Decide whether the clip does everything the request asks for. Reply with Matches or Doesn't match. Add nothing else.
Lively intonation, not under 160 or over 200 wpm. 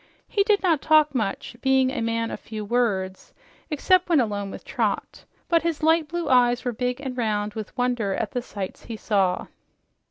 Matches